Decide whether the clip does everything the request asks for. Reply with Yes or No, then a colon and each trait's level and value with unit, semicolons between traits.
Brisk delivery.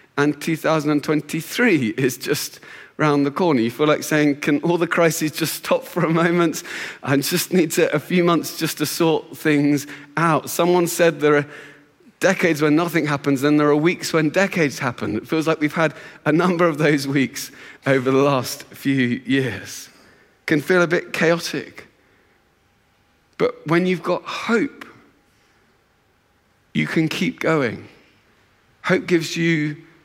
No: average, 160 wpm